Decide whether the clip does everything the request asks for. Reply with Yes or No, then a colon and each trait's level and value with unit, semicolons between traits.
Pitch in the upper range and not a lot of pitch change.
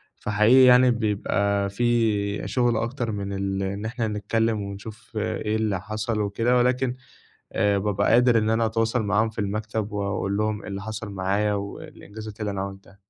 No: low, 105 Hz; narrow, 2.1 semitones